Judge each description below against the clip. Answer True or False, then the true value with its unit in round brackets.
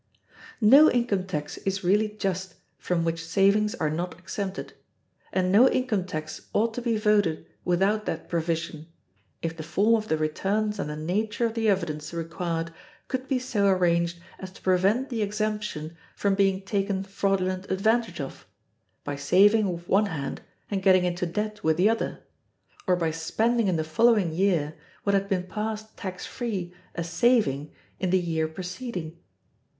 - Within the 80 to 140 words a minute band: False (165 wpm)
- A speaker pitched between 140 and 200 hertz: True (190 Hz)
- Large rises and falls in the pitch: False (4.0 semitones)